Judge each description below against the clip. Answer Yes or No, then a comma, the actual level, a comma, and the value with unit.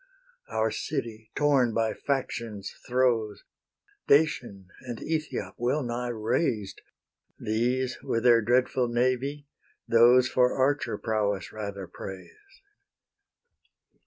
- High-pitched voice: No, low, 120 Hz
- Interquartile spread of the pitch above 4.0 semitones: No, average, 2.9 semitones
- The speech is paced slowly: Yes, slow, 100 wpm